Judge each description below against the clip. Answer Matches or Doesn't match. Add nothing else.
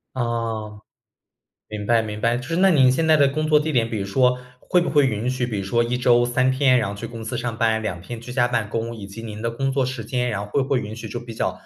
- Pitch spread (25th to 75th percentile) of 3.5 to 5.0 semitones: Doesn't match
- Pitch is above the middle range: Doesn't match